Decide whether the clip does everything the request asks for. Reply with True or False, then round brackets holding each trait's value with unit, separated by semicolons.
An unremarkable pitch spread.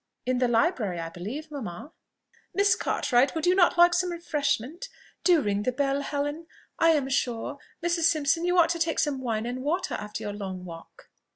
False (6.5 semitones)